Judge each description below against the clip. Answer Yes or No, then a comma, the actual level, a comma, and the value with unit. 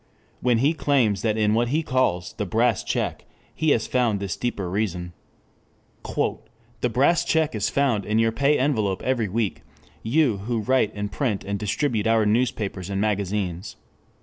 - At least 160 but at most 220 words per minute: Yes, average, 170 wpm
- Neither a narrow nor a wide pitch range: Yes, average, 3.9 semitones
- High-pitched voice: No, low, 110 Hz